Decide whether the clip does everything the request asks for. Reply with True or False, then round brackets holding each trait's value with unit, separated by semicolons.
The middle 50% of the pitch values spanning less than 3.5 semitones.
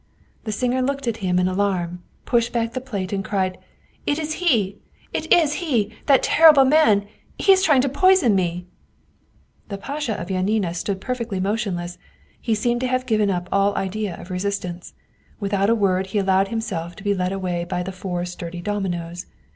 False (4.7 semitones)